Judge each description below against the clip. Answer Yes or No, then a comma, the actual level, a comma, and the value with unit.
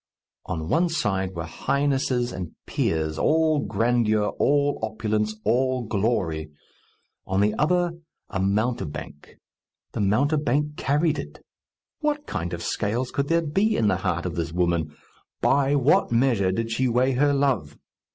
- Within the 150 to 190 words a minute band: No, average, 140 wpm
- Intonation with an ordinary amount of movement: No, wide, 7.0 semitones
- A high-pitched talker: No, low, 115 Hz